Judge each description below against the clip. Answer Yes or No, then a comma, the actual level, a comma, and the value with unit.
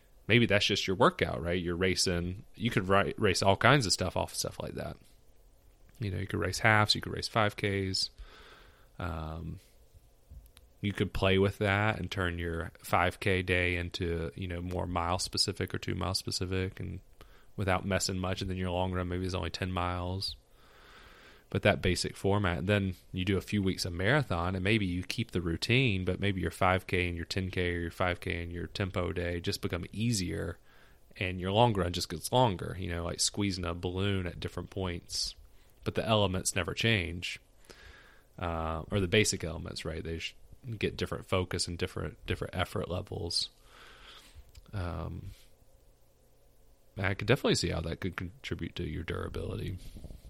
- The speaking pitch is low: Yes, very low, 90 Hz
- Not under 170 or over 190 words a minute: Yes, average, 180 wpm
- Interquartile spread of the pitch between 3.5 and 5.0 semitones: No, narrow, 2.4 semitones